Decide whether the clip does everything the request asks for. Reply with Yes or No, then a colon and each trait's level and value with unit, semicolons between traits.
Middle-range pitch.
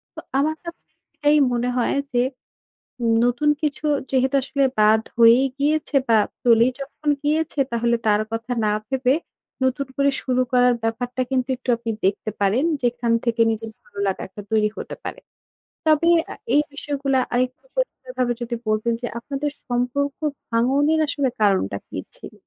No: very high, 250 Hz